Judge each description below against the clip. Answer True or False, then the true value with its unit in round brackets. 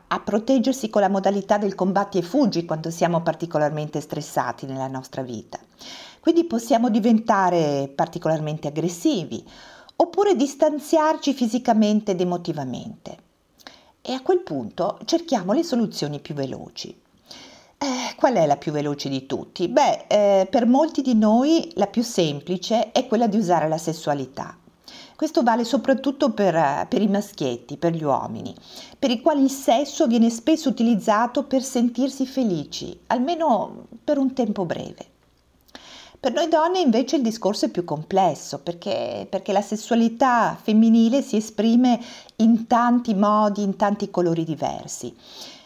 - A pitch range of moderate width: False (7.3 semitones)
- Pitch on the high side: True (215 Hz)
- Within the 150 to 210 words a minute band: False (140 wpm)